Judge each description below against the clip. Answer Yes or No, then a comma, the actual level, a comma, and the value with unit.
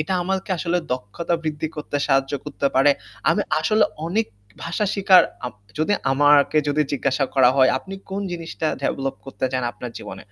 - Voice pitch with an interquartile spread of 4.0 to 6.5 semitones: Yes, average, 4.4 semitones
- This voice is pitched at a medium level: Yes, medium, 150 Hz